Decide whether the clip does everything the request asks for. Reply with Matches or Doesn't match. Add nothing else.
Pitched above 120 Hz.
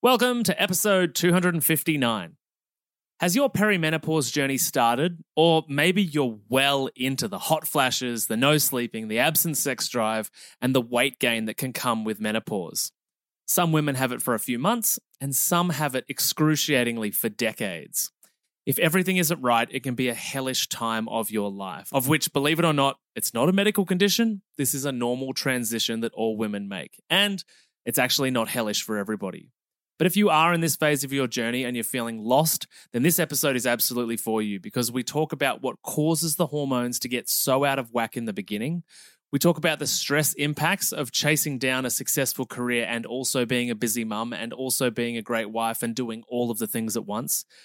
Matches